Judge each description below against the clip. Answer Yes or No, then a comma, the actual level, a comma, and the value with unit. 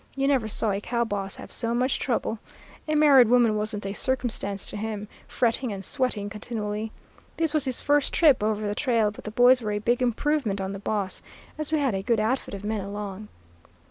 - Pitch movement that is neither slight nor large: Yes, average, 3.7 semitones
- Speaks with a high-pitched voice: Yes, high, 220 Hz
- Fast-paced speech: Yes, fast, 210 wpm